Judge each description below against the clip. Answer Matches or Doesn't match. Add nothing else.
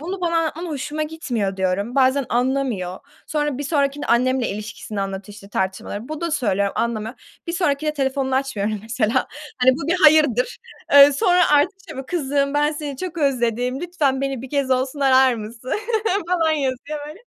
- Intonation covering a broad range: Doesn't match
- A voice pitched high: Matches